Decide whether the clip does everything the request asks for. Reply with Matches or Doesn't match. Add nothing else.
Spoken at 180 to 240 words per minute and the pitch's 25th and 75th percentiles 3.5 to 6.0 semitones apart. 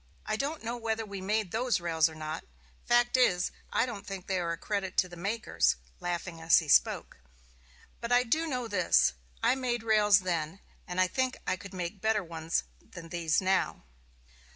Matches